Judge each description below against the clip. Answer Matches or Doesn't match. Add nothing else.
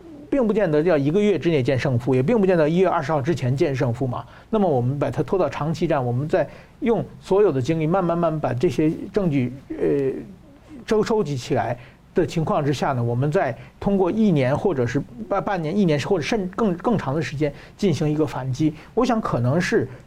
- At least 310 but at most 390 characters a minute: Matches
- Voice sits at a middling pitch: Matches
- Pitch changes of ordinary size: Doesn't match